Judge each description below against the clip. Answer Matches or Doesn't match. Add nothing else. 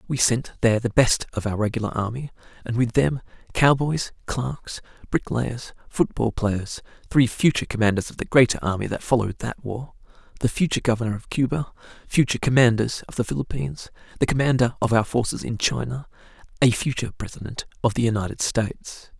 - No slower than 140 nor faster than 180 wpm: Matches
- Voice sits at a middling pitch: Doesn't match